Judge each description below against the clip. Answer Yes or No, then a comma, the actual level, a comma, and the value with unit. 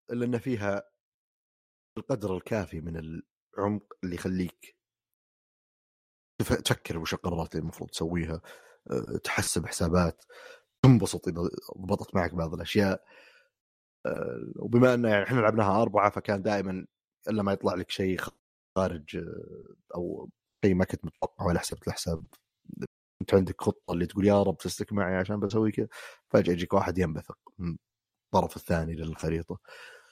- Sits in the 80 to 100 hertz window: Yes, very low, 95 Hz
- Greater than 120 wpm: Yes, average, 130 wpm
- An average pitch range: Yes, average, 3.4 semitones